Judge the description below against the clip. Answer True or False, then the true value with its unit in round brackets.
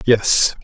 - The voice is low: True (110 Hz)